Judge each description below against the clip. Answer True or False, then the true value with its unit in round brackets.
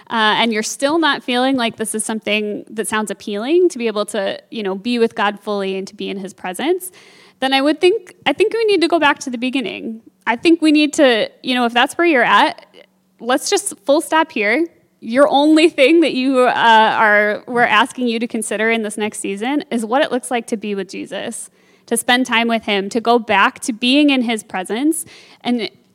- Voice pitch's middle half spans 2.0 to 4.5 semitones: False (5.0 semitones)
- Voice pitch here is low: False (240 Hz)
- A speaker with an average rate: False (230 wpm)